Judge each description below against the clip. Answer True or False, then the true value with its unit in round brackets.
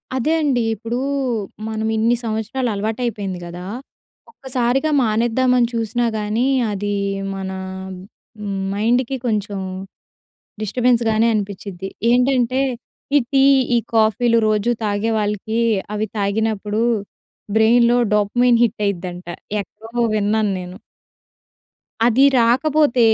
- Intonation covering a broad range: False (2.8 semitones)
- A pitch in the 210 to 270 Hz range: True (225 Hz)